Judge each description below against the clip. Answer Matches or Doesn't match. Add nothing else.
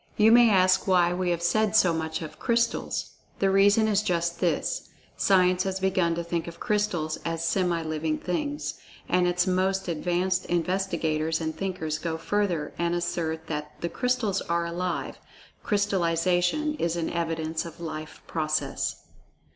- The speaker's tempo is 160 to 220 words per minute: Doesn't match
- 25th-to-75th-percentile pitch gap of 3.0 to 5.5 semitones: Doesn't match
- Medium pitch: Matches